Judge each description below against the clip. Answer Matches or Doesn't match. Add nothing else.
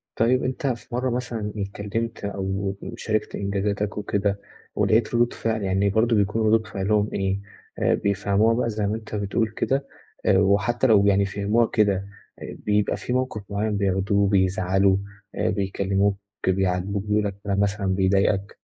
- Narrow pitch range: Matches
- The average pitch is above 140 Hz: Doesn't match